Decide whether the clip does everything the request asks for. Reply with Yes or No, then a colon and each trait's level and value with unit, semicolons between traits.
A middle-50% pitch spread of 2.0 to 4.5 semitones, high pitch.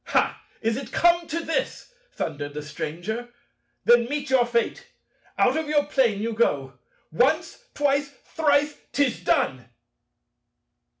No: average, 5.2 semitones; very high, 260 Hz